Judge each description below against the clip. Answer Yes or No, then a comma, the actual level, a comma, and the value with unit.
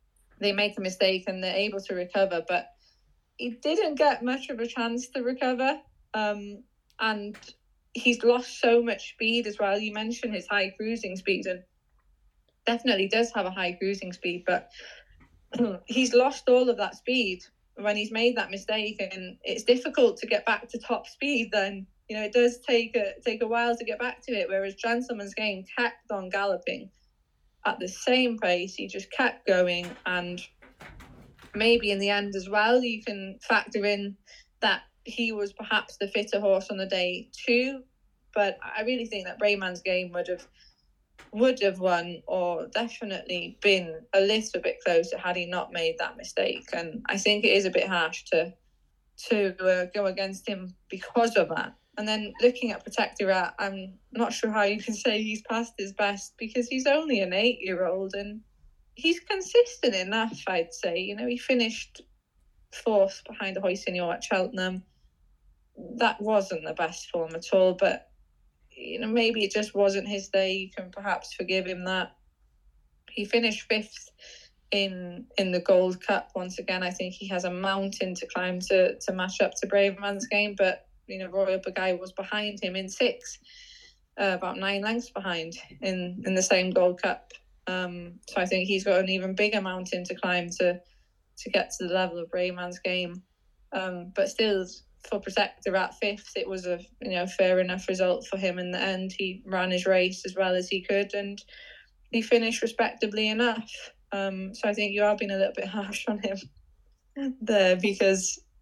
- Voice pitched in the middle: No, high, 200 Hz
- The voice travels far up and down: No, average, 3.8 semitones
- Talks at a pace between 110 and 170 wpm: No, average, 185 wpm